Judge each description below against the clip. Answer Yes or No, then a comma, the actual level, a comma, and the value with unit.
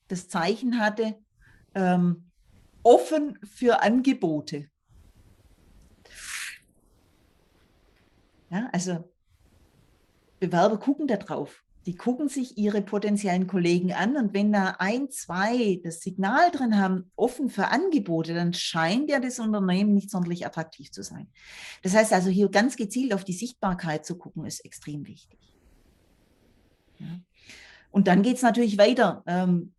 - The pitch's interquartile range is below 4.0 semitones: No, average, 4.6 semitones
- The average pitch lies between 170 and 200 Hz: Yes, high, 190 Hz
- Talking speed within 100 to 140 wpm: Yes, average, 130 wpm